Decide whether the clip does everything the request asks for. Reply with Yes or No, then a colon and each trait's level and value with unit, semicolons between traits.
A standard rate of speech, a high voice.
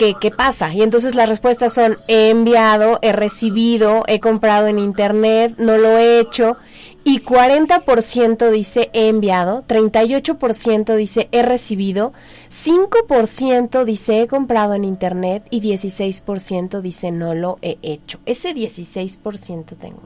Yes: average, 135 wpm; high, 220 Hz